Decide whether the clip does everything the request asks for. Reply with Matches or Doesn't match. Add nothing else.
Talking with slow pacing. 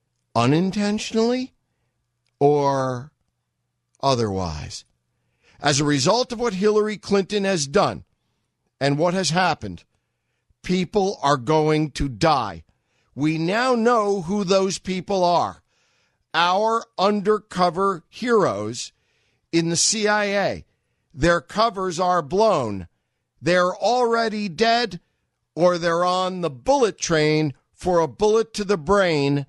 Matches